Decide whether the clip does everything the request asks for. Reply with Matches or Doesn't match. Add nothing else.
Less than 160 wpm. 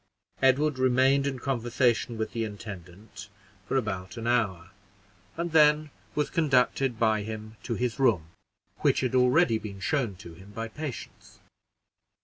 Matches